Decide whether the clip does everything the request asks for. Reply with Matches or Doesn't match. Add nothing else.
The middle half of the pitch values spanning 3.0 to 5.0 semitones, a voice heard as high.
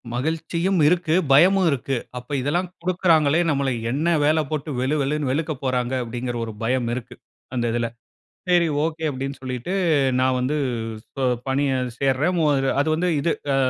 Doesn't match